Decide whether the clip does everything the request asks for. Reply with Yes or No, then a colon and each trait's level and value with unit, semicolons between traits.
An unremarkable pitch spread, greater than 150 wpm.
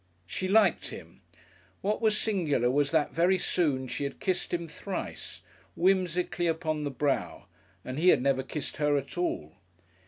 Yes: average, 4.6 semitones; average, 160 wpm